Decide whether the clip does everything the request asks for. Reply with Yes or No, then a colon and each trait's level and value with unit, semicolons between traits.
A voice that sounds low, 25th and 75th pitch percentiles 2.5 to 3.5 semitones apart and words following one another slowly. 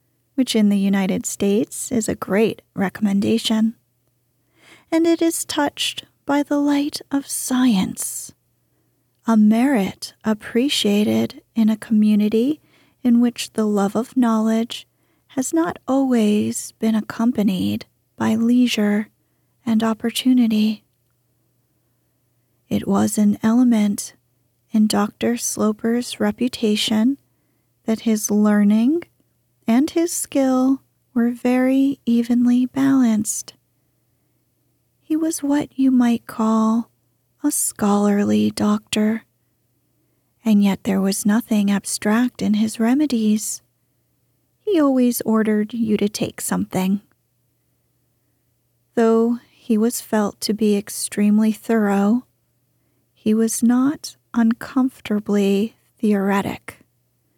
No: high, 220 Hz; average, 3.2 semitones; slow, 100 wpm